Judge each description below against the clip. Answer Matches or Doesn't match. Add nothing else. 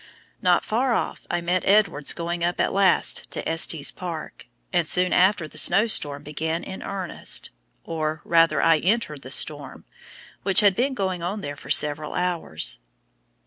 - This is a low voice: Doesn't match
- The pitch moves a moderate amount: Matches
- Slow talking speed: Doesn't match